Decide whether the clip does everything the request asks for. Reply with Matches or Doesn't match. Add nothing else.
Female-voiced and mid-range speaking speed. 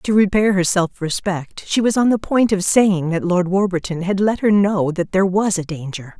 Doesn't match